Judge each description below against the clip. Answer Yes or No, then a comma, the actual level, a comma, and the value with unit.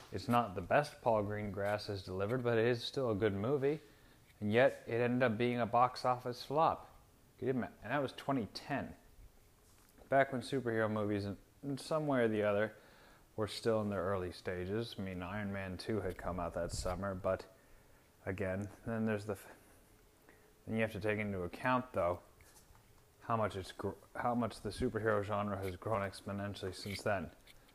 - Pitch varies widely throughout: No, average, 3.3 semitones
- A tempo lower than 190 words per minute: Yes, average, 180 wpm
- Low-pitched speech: Yes, low, 105 Hz